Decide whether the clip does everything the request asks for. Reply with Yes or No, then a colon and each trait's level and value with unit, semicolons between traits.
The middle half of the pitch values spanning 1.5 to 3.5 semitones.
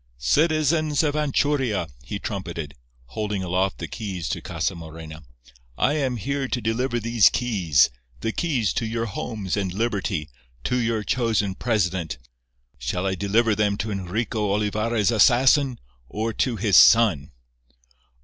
No: average, 4.5 semitones